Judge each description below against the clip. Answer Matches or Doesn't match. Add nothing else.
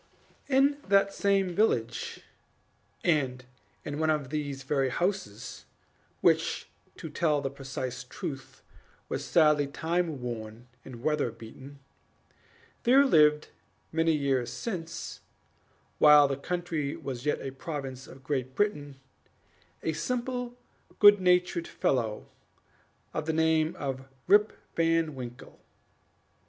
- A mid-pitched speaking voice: Matches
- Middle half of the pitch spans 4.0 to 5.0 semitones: Matches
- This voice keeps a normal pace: Doesn't match